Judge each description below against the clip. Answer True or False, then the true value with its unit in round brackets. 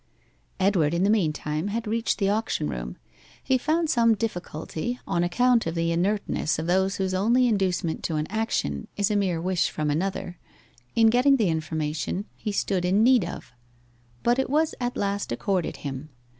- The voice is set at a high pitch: True (195 Hz)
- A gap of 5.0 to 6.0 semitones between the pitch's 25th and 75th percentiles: True (5.3 semitones)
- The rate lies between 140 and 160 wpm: False (175 wpm)